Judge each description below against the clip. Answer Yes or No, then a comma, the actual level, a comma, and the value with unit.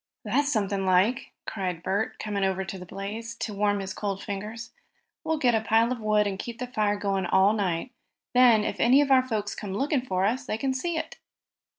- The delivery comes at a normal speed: No, fast, 215 wpm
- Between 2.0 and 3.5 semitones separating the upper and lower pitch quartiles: No, average, 3.9 semitones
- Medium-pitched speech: No, high, 210 Hz